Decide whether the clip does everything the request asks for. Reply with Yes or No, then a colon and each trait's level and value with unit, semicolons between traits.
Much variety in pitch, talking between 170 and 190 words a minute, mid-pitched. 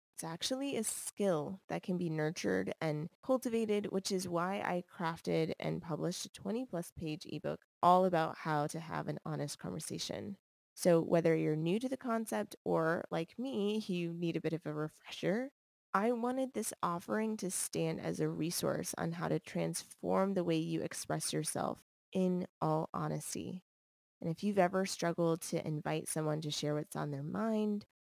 No: average, 4.0 semitones; average, 175 wpm; medium, 170 Hz